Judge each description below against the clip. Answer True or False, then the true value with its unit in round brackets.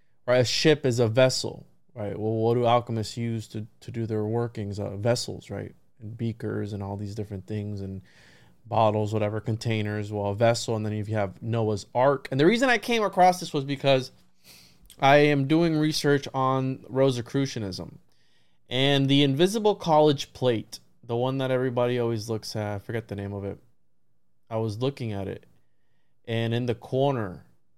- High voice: False (115 Hz)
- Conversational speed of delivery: True (175 wpm)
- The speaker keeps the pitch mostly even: False (4.2 semitones)